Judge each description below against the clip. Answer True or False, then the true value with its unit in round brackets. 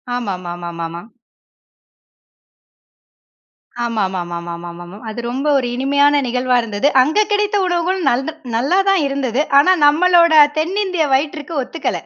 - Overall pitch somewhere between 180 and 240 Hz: False (270 Hz)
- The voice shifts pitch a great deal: True (8.6 semitones)